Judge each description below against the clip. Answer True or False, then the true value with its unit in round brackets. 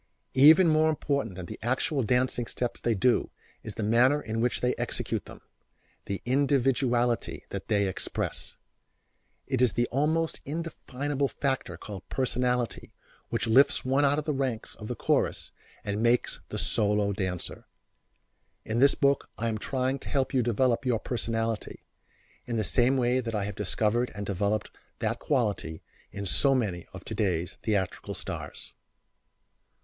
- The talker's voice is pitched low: True (120 Hz)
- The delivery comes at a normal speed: True (155 wpm)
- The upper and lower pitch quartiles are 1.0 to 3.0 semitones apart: False (4.0 semitones)